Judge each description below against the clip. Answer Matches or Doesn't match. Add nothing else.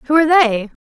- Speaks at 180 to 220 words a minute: Matches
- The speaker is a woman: Matches